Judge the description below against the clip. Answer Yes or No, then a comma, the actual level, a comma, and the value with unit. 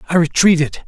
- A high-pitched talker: No, medium, 165 Hz